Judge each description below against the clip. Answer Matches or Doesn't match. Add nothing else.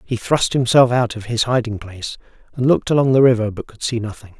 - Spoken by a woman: Doesn't match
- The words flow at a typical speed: Doesn't match